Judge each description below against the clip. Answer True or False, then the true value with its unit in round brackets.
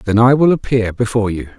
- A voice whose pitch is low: True (115 Hz)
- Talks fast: True (225 wpm)